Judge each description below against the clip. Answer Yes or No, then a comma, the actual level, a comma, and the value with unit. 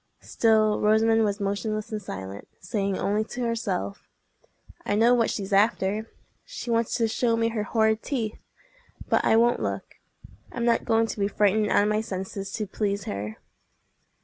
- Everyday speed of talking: Yes, average, 170 wpm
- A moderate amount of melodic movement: No, narrow, 2.2 semitones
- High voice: Yes, high, 215 Hz